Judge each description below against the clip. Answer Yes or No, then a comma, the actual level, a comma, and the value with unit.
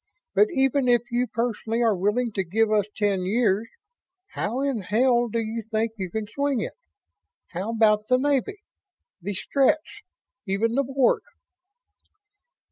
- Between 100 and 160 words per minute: Yes, average, 145 wpm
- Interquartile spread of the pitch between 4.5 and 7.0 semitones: No, average, 3.2 semitones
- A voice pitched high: Yes, high, 230 Hz